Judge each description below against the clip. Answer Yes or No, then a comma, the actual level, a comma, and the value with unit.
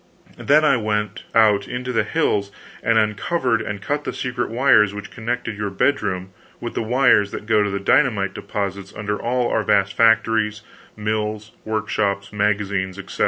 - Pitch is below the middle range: Yes, low, 105 Hz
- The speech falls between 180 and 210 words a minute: No, average, 165 wpm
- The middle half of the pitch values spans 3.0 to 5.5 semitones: No, narrow, 2.5 semitones